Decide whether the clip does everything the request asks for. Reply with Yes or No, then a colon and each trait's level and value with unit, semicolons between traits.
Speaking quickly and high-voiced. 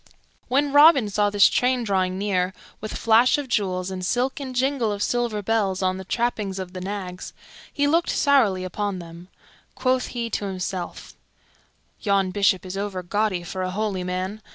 No: average, 170 wpm; high, 205 Hz